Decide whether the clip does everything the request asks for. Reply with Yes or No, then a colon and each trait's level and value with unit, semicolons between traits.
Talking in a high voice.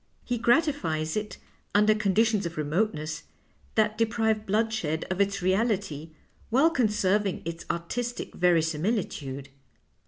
Yes: high, 205 Hz